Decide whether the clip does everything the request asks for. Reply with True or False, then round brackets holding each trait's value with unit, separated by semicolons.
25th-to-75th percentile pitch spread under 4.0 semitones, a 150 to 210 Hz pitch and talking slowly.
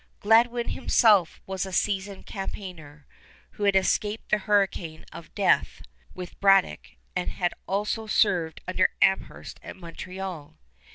True (2.4 semitones; 190 Hz; 125 wpm)